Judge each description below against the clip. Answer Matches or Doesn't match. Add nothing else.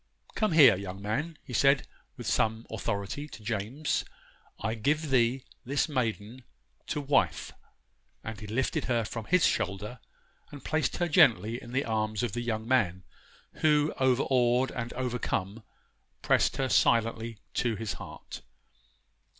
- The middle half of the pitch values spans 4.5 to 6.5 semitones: Doesn't match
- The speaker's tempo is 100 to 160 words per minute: Matches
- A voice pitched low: Matches